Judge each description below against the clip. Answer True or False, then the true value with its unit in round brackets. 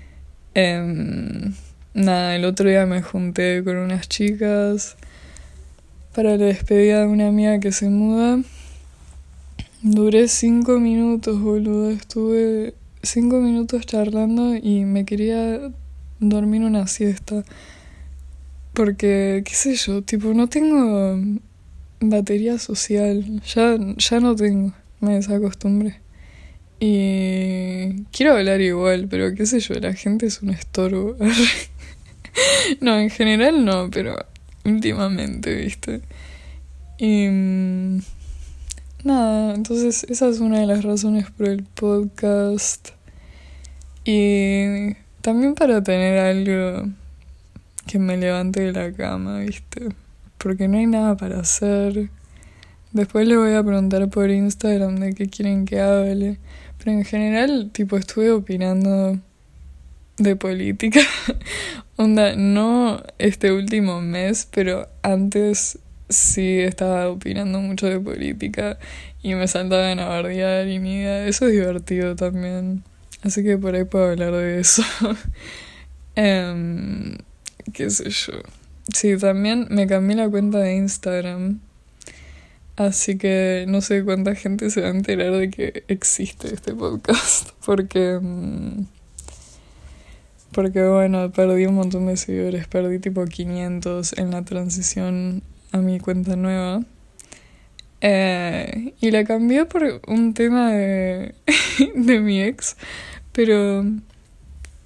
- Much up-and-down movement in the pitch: False (2.7 semitones)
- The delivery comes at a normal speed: False (120 wpm)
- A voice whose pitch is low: False (195 Hz)